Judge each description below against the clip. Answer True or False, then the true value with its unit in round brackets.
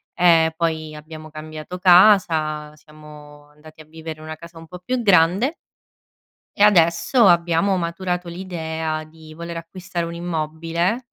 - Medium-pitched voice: True (165 Hz)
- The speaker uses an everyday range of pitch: False (2.2 semitones)